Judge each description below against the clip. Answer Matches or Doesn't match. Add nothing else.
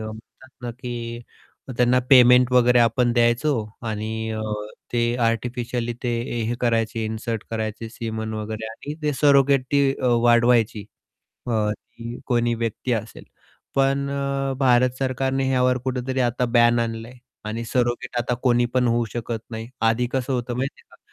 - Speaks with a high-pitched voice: Doesn't match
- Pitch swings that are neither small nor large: Doesn't match